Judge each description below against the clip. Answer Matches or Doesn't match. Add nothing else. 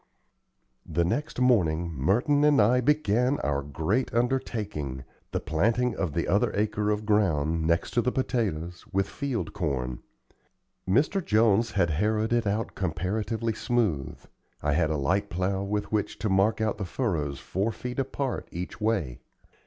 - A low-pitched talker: Matches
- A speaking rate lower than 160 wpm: Matches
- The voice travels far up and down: Matches